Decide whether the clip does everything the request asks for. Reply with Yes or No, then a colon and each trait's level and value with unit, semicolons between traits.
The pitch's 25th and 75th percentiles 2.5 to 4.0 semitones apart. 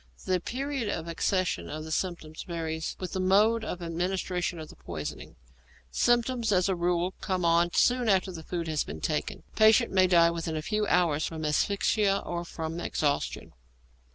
Yes: average, 3.4 semitones